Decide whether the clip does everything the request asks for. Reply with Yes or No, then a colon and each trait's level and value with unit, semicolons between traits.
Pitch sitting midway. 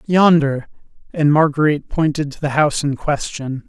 Yes: medium, 150 Hz